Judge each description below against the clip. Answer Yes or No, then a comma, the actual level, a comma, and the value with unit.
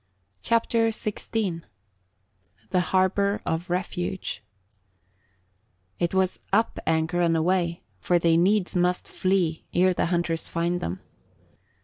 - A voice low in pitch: No, medium, 180 Hz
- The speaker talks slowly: Yes, slow, 110 wpm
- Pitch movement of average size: No, narrow, 2.0 semitones